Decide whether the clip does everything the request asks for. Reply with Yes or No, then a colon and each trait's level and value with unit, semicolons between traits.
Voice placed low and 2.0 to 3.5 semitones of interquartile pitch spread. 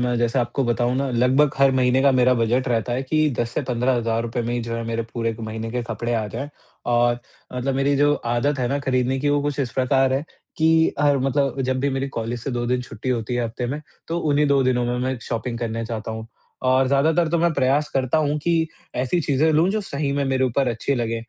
Yes: low, 130 Hz; average, 2.8 semitones